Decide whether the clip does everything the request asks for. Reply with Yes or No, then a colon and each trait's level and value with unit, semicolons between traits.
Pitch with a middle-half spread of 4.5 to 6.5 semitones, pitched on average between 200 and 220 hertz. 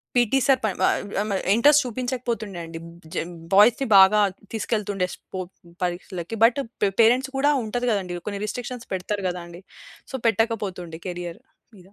Yes: average, 4.9 semitones; high, 210 Hz